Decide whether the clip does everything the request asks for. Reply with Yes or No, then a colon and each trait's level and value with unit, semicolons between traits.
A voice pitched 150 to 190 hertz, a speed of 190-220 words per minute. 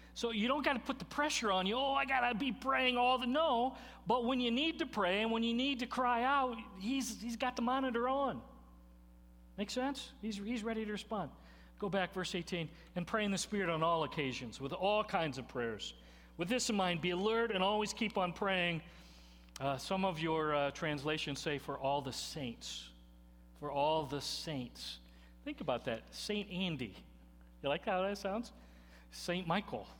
Yes: medium, 185 Hz; average, 200 wpm